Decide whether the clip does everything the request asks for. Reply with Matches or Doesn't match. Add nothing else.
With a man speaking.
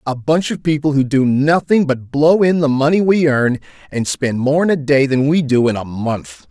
Matches